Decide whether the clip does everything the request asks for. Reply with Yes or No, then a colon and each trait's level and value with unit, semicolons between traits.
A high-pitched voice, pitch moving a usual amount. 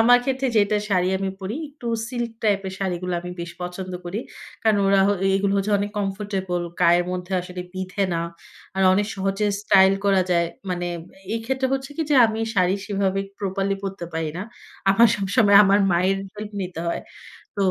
No: high, 195 Hz; narrow, 2.2 semitones